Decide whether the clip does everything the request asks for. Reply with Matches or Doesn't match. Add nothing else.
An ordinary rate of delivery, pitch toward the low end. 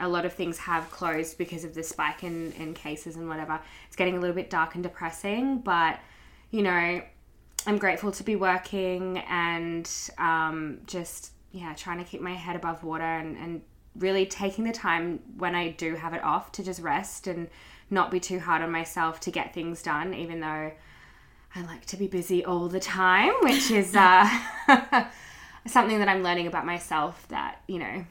Doesn't match